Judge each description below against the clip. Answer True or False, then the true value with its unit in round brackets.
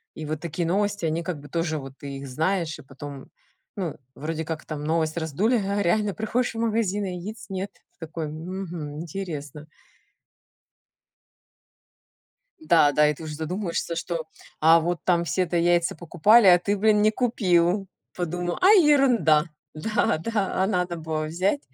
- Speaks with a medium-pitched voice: True (170 Hz)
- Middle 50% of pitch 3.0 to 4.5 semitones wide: True (4.2 semitones)